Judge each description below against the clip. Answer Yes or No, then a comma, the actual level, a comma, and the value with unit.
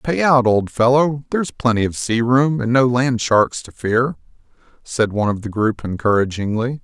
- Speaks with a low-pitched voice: Yes, low, 120 Hz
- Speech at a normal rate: Yes, average, 185 wpm